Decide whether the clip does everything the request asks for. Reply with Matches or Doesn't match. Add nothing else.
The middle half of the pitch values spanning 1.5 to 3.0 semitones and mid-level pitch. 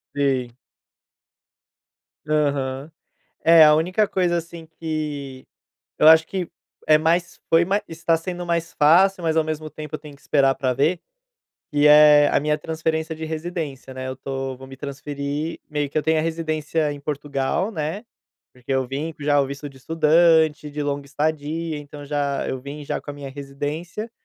Matches